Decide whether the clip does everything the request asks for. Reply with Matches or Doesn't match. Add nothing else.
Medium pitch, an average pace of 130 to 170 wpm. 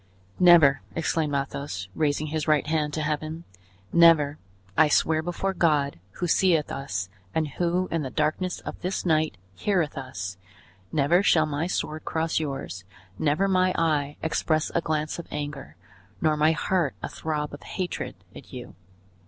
Matches